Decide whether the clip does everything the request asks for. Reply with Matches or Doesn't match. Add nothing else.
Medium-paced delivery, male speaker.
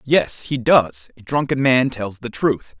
Matches